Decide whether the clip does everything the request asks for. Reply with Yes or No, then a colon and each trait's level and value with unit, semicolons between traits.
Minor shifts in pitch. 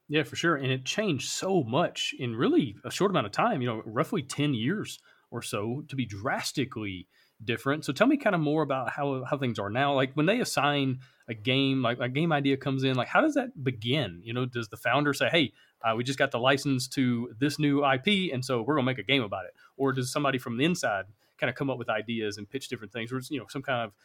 No: average, 3.1 semitones